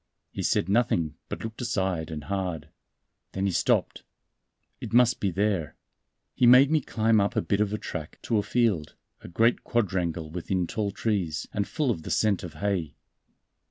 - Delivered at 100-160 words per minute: No, average, 180 wpm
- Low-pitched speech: Yes, low, 100 Hz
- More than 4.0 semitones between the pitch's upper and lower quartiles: Yes, average, 4.6 semitones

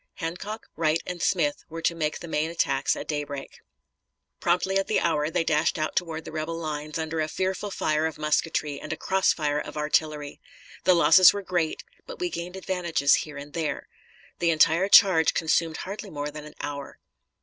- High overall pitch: No, medium, 160 Hz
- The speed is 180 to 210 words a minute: Yes, average, 190 wpm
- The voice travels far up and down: No, average, 2.7 semitones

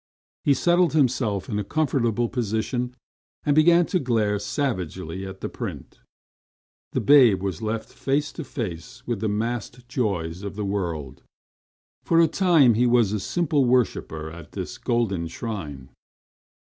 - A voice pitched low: Yes, low, 115 Hz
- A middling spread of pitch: No, wide, 5.8 semitones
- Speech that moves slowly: No, average, 145 wpm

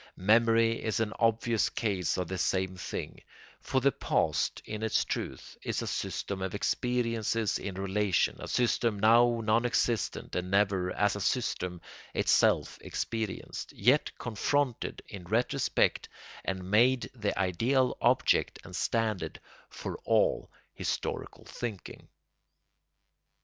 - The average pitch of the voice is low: Yes, low, 110 Hz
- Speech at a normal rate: No, slow, 125 wpm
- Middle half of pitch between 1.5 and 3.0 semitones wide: No, average, 3.4 semitones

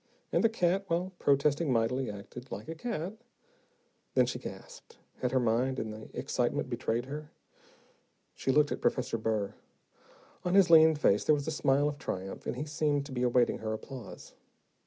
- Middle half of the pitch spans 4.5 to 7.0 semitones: Yes, average, 5.0 semitones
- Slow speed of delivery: No, average, 180 wpm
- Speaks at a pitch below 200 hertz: Yes, medium, 140 Hz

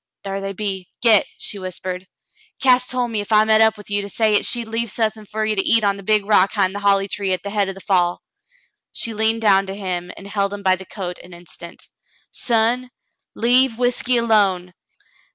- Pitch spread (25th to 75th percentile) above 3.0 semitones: No, narrow, 2.5 semitones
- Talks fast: Yes, fast, 220 wpm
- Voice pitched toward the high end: Yes, high, 205 Hz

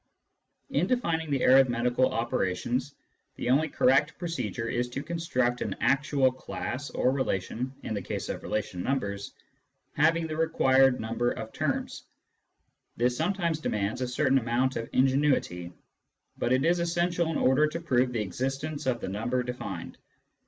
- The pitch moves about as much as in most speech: Yes, average, 4.1 semitones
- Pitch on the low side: Yes, low, 130 Hz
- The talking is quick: No, average, 150 wpm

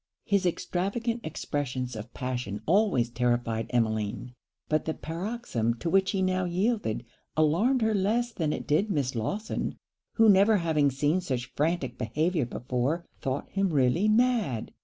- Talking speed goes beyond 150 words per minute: No, average, 145 wpm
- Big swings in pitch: Yes, wide, 8.0 semitones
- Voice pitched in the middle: Yes, medium, 160 Hz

